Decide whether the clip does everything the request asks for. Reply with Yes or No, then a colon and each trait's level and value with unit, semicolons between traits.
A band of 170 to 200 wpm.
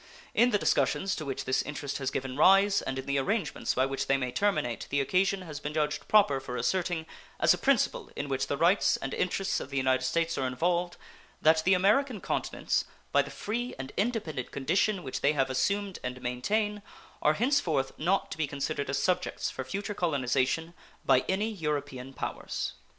Yes: average, 190 wpm